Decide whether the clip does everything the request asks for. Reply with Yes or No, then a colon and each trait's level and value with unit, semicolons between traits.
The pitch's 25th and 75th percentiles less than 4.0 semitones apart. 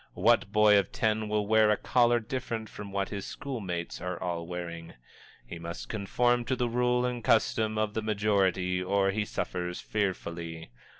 Yes: average, 3.4 semitones